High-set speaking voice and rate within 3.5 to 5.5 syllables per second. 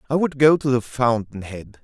No: low, 125 Hz; 5.0 syllables/s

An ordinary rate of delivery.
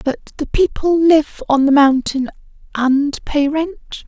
Yes: average, 145 wpm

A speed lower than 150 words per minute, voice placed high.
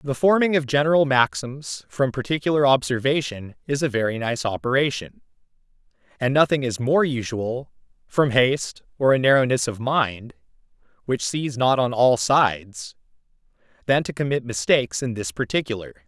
No: average, 140 wpm; low, 125 Hz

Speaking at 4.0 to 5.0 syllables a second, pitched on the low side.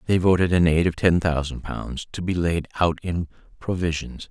Yes: 4.9 syllables/s; very low, 85 Hz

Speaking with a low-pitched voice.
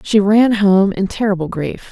No: high, 200 Hz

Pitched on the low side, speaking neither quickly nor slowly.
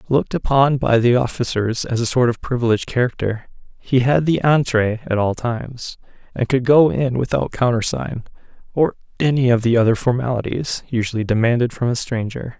Yes: low, 120 Hz; average, 165 wpm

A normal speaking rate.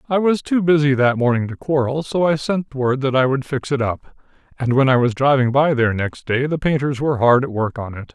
No: fast, 260 wpm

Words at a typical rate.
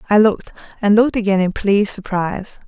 Yes: average, 180 wpm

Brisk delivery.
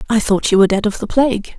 Yes: fast, 305 wpm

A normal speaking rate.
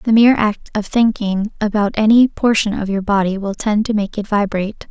No: fast, 210 wpm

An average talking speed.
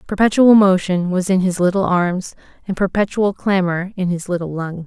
Yes: average, 175 wpm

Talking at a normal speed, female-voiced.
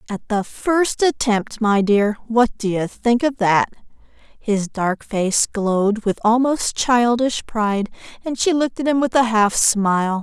Yes: average, 170 wpm; female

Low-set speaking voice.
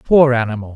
Yes: low, 125 Hz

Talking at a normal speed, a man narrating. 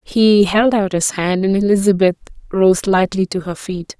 No: average, 180 wpm; female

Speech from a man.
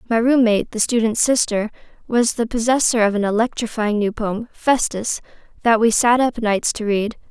No: female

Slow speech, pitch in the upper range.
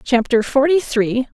Yes: slow, 130 wpm; very high, 255 Hz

